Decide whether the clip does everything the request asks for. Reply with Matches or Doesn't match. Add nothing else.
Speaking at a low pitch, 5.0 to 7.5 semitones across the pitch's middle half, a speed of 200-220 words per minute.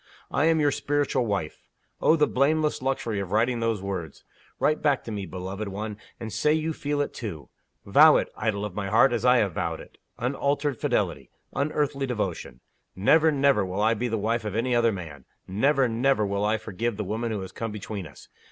Matches